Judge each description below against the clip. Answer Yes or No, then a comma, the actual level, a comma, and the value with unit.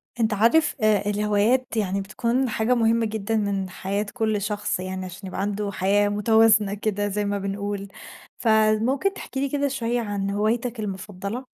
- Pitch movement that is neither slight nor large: No, narrow, 2.3 semitones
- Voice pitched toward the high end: Yes, high, 210 Hz